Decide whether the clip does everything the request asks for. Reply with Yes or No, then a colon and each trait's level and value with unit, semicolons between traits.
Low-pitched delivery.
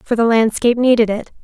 No: high, 230 Hz